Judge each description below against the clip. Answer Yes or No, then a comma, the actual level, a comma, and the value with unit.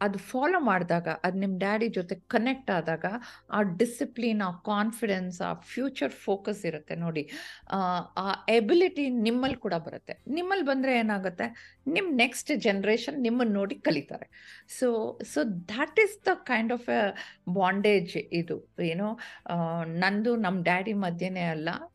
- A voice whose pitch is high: Yes, high, 215 Hz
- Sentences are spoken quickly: Yes, fast, 130 wpm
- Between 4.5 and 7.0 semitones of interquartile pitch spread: Yes, average, 5.2 semitones